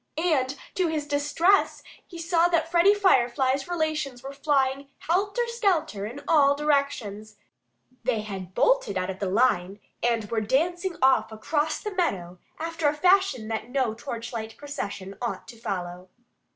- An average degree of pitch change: No, wide, 7.1 semitones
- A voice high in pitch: Yes, very high, 275 Hz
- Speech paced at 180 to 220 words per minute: No, average, 150 wpm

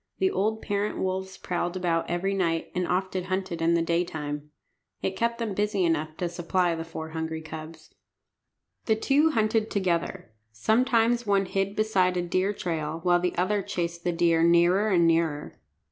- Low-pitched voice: No, medium, 180 Hz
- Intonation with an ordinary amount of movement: Yes, average, 3.2 semitones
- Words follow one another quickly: No, average, 170 wpm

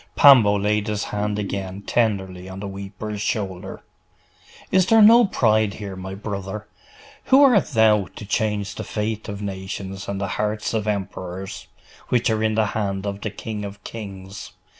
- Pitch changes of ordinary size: No, narrow, 1.9 semitones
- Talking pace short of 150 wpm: No, average, 165 wpm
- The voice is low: Yes, low, 105 Hz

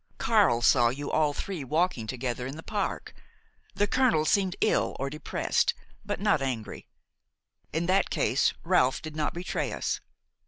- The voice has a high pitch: No, medium, 155 Hz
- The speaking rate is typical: Yes, average, 160 wpm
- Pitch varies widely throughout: Yes, wide, 6.1 semitones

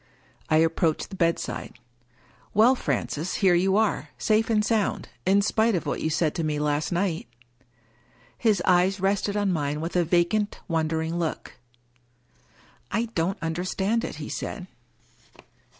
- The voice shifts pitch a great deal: No, average, 4.1 semitones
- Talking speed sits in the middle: Yes, average, 150 wpm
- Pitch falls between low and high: Yes, medium, 175 Hz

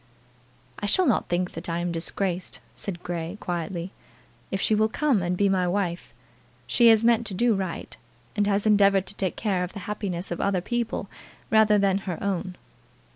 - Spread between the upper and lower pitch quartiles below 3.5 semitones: Yes, average, 2.9 semitones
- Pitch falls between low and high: No, high, 195 Hz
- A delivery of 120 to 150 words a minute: No, average, 185 wpm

